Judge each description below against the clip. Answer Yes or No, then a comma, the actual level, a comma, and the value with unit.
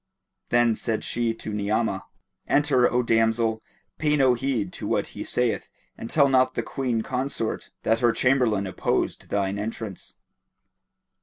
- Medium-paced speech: Yes, average, 145 wpm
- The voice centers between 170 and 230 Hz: No, low, 115 Hz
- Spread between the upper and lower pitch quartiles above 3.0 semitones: No, average, 2.7 semitones